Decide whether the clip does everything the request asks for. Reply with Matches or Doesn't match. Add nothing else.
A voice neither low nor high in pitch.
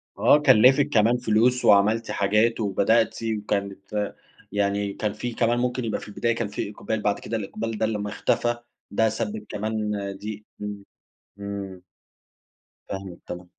Doesn't match